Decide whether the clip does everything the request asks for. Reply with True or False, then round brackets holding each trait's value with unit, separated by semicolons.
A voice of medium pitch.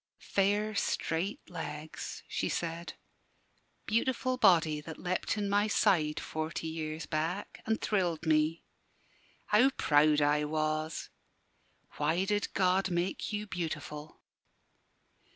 True (170 Hz)